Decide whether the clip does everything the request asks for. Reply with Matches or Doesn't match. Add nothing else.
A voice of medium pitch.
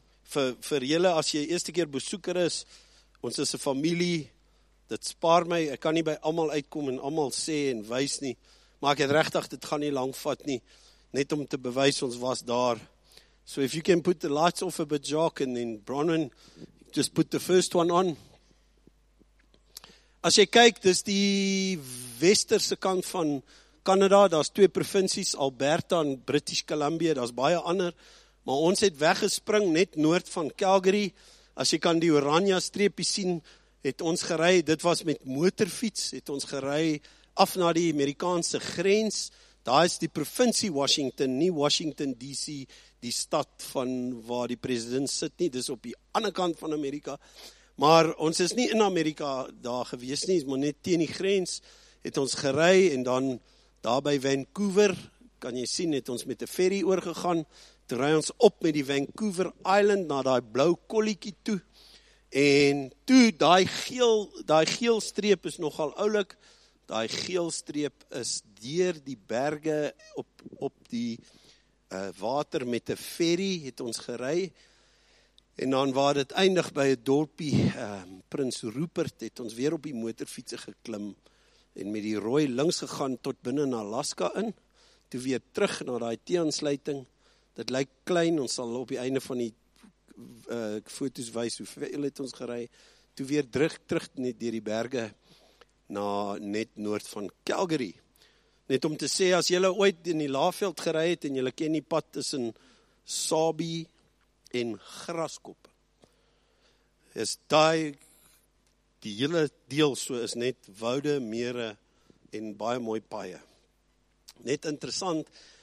Matches